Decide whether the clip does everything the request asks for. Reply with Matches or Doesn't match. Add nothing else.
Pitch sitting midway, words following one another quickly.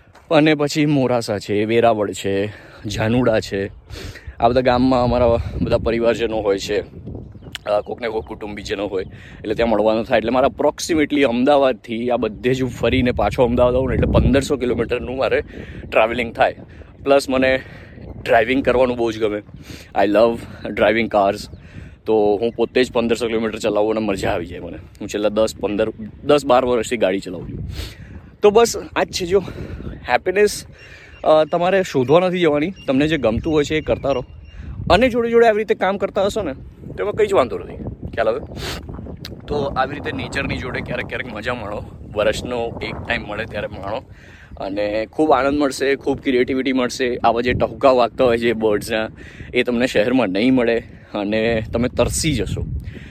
Doesn't match